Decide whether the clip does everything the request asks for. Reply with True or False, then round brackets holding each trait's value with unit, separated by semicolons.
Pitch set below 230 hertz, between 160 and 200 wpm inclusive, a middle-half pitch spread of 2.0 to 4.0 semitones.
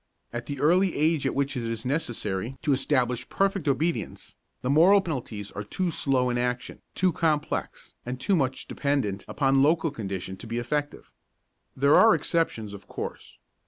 False (135 Hz; 165 wpm; 4.9 semitones)